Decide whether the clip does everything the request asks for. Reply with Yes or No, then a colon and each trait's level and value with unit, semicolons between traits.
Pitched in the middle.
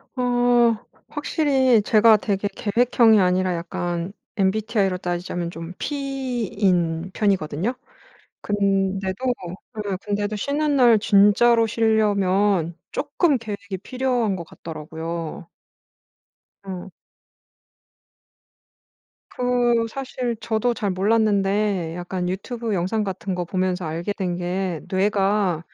No: high, 200 Hz